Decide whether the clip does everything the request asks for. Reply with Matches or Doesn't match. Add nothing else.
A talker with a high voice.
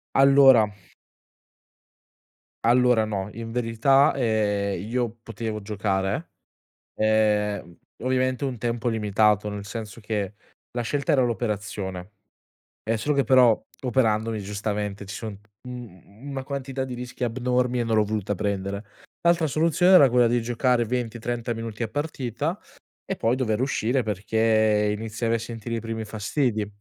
Doesn't match